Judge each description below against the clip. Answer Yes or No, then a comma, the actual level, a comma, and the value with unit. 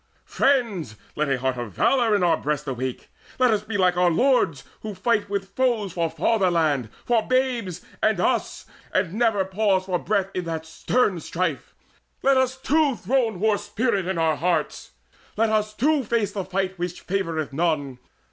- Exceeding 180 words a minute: No, average, 175 wpm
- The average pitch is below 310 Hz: Yes, high, 190 Hz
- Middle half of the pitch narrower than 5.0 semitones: No, wide, 5.4 semitones